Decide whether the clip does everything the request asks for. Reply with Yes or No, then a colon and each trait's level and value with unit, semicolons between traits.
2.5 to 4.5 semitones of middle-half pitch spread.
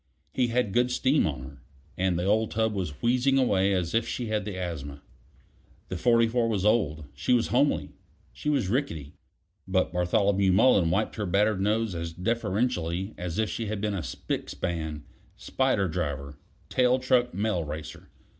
No: average, 5.2 semitones